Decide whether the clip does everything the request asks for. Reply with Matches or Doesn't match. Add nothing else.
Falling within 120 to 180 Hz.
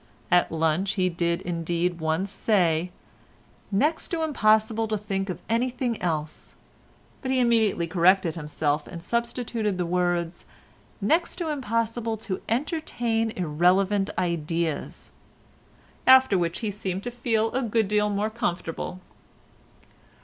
Doesn't match